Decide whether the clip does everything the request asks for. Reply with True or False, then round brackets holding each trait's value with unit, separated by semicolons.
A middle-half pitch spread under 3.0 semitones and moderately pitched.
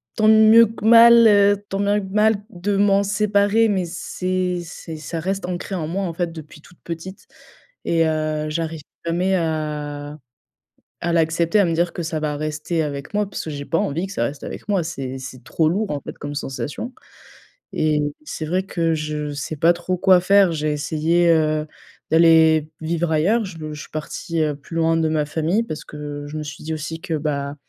False (3.7 semitones; 165 Hz)